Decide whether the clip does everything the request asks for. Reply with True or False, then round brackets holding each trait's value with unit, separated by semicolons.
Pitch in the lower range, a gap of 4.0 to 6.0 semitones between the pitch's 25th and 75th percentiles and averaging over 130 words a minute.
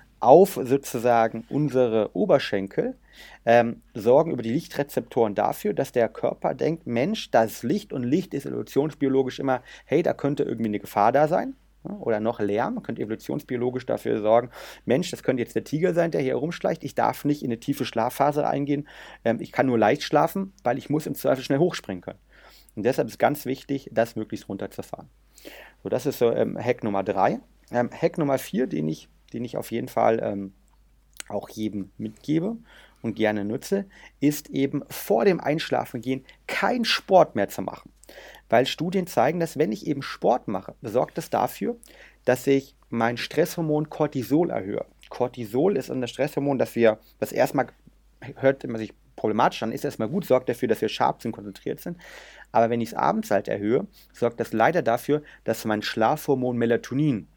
True (125 Hz; 4.5 semitones; 180 wpm)